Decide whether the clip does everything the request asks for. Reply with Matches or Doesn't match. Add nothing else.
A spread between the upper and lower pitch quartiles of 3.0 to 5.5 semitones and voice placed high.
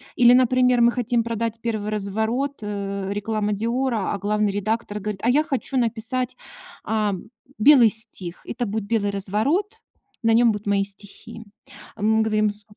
Doesn't match